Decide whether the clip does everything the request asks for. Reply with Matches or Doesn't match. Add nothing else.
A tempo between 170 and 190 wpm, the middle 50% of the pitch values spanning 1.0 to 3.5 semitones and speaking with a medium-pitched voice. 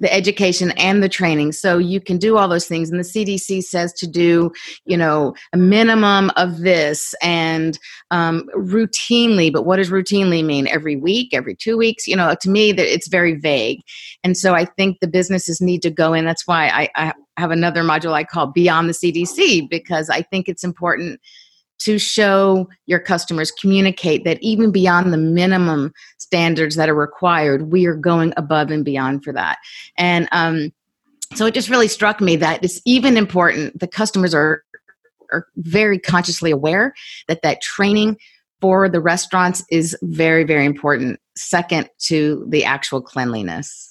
Matches